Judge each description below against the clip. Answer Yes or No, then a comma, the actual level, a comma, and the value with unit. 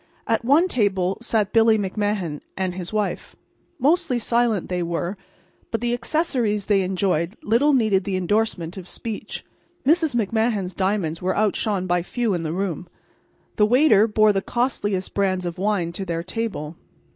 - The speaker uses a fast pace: No, average, 155 wpm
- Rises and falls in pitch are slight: No, average, 3.8 semitones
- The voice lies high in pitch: Yes, high, 205 Hz